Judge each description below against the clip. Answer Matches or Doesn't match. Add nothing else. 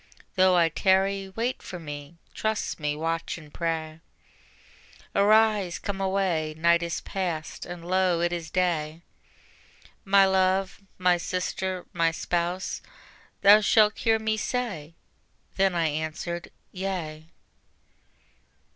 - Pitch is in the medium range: Matches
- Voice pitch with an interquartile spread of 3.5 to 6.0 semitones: Doesn't match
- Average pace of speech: Doesn't match